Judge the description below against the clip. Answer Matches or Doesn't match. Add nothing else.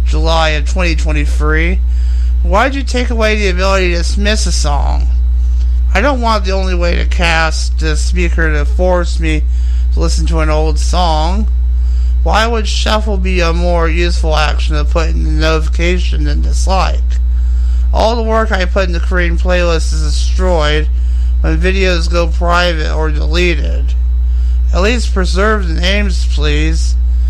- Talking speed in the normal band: Matches